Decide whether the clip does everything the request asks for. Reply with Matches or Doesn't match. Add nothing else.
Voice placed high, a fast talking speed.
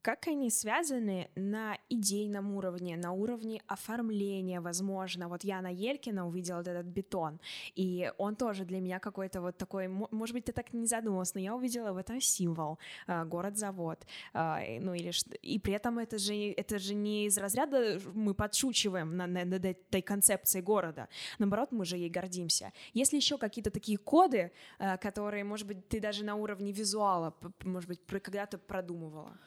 Matches